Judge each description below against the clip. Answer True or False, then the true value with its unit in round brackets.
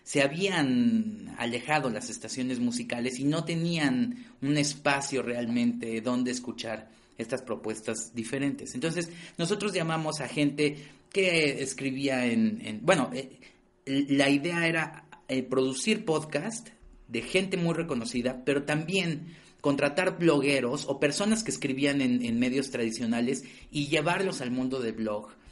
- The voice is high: False (140 Hz)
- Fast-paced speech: False (130 wpm)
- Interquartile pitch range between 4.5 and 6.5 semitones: True (5.1 semitones)